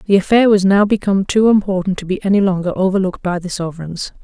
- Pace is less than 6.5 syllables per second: No, 6.6 syllables/s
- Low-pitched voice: No, high, 190 Hz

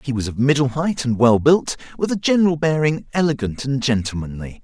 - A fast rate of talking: No, average, 195 wpm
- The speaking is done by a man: Yes, male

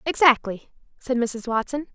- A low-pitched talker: No, very high, 255 Hz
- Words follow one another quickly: No, slow, 125 wpm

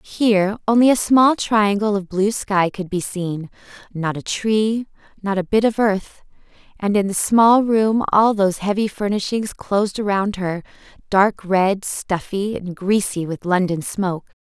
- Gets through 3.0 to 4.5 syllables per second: Yes, 4.2 syllables/s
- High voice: Yes, high, 200 Hz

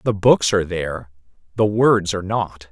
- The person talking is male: Yes, male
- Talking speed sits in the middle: Yes, average, 155 wpm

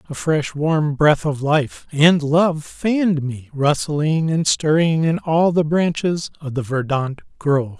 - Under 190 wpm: Yes, average, 160 wpm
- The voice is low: No, medium, 150 Hz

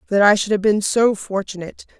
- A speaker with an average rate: No, fast, 210 wpm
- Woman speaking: Yes, female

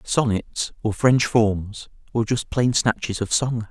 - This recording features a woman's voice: No, male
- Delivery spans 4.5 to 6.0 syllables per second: No, 3.7 syllables/s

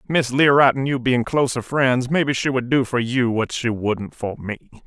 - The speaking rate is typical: No, fast, 220 wpm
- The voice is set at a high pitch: No, low, 125 Hz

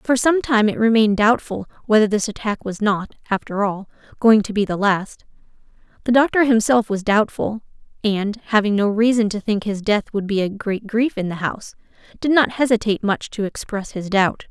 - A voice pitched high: Yes, high, 215 Hz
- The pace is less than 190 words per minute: No, average, 195 wpm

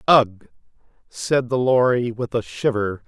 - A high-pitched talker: No, low, 115 Hz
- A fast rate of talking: No, slow, 135 wpm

